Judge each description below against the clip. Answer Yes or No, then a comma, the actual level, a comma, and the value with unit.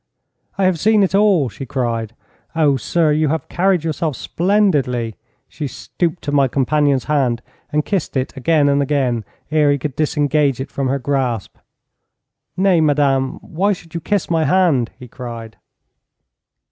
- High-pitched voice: No, medium, 145 Hz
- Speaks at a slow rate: No, average, 160 wpm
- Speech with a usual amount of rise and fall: Yes, average, 4.1 semitones